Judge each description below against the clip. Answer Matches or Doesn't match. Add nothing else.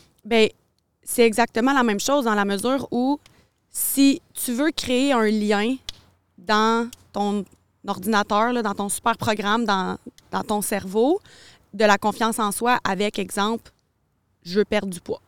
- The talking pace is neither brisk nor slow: Matches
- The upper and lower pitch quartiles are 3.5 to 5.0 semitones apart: Doesn't match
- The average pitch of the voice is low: Doesn't match